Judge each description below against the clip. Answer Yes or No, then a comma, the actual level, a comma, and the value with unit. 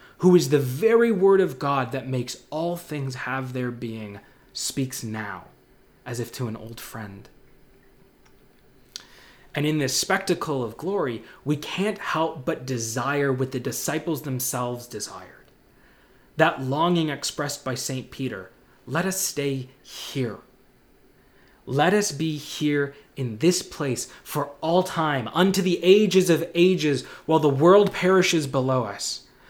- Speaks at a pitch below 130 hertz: No, medium, 140 Hz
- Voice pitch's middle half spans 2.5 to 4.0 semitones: No, average, 4.8 semitones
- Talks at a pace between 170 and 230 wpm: No, average, 140 wpm